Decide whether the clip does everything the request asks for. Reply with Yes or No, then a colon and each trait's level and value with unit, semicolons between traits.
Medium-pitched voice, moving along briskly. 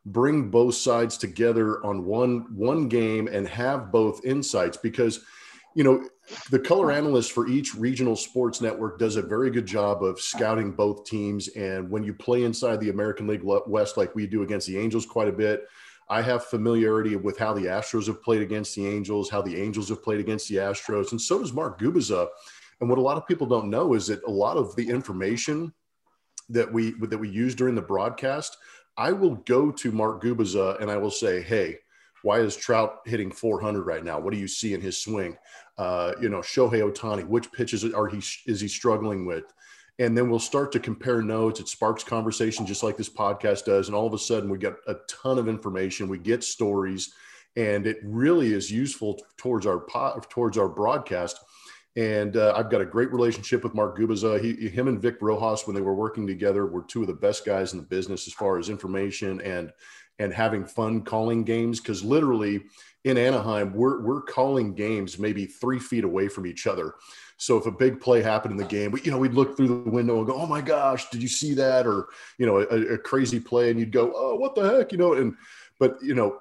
No: low, 110 Hz; fast, 215 wpm